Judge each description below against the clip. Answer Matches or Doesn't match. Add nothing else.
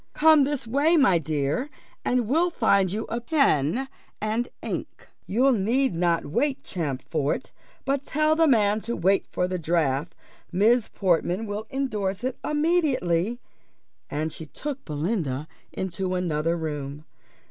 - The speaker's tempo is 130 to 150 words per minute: Matches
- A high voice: Matches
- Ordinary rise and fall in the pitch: Doesn't match